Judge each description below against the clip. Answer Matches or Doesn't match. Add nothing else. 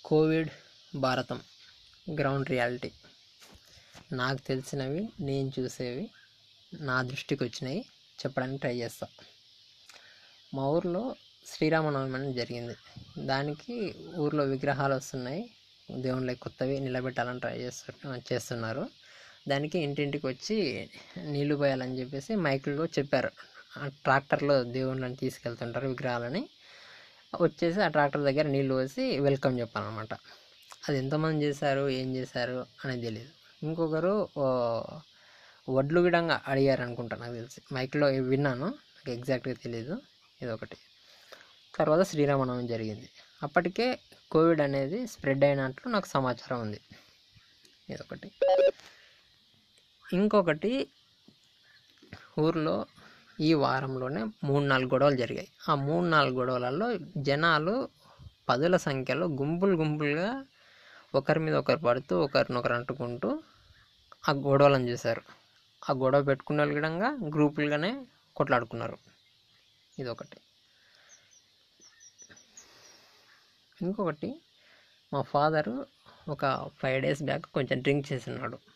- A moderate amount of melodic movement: Matches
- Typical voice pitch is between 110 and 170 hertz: Matches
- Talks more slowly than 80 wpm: Doesn't match